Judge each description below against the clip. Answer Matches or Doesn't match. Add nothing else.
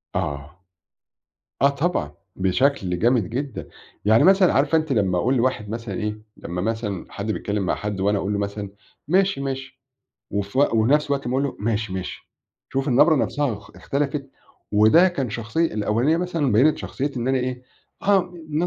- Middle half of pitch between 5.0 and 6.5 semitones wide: Matches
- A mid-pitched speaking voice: Doesn't match